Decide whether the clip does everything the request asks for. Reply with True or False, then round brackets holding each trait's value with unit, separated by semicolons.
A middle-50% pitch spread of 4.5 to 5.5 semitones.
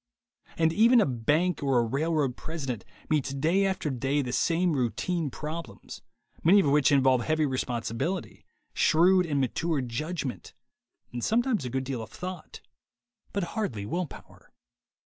True (5.1 semitones)